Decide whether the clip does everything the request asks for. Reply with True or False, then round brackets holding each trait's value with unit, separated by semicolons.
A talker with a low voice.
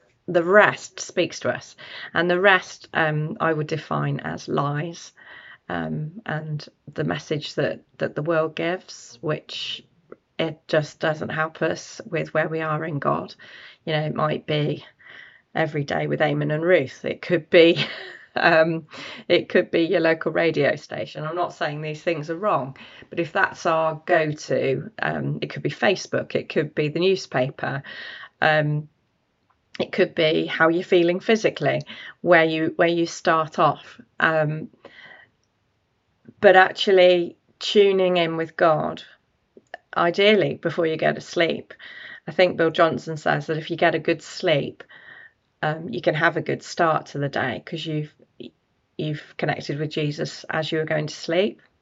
False (160 Hz)